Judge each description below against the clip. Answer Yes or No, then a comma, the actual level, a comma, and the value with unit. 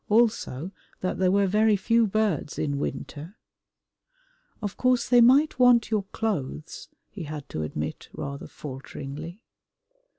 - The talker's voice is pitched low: No, high, 190 Hz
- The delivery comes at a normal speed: No, slow, 130 wpm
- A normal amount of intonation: No, wide, 7.4 semitones